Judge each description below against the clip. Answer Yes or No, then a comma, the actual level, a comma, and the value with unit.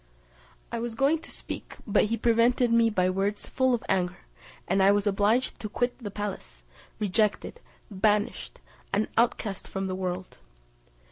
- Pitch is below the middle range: No, high, 210 Hz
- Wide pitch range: No, average, 3.2 semitones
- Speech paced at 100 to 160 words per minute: Yes, average, 155 wpm